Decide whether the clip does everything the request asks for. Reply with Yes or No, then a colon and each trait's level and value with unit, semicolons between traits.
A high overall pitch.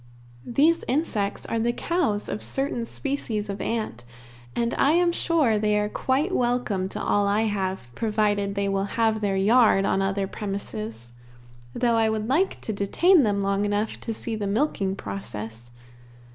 Yes: high, 210 Hz